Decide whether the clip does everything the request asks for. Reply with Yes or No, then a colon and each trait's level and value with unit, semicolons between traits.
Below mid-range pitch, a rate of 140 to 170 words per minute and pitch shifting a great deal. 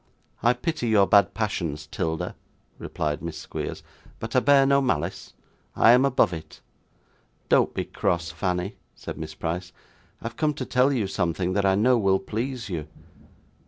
Yes: low, 100 Hz; average, 165 wpm; wide, 6.6 semitones